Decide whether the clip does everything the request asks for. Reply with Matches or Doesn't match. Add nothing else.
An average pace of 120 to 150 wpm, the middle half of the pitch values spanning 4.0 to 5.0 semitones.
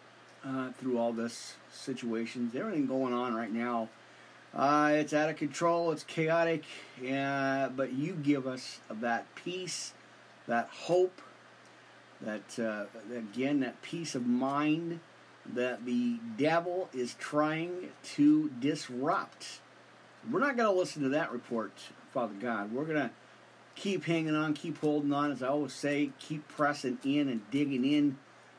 Matches